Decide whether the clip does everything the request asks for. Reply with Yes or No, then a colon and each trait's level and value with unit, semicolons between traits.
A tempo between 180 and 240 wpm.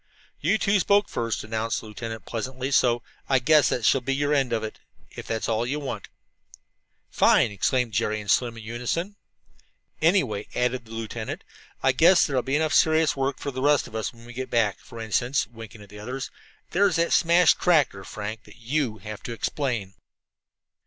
Yes: average, 195 wpm